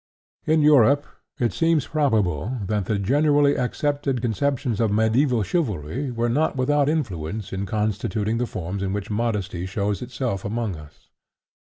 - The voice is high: No, low, 115 Hz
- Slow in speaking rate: No, average, 145 wpm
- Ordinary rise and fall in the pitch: No, wide, 5.9 semitones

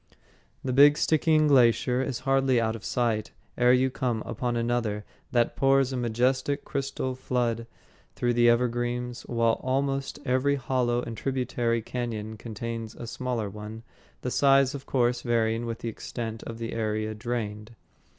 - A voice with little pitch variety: Yes, narrow, 2.2 semitones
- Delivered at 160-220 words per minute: No, average, 150 wpm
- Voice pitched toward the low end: Yes, low, 120 Hz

